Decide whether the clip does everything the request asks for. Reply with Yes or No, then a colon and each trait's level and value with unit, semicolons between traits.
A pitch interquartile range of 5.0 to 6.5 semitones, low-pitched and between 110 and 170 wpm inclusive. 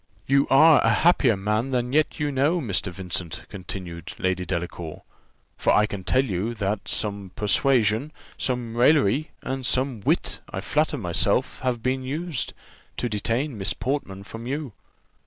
Yes: wide, 5.5 semitones; low, 115 Hz; average, 155 wpm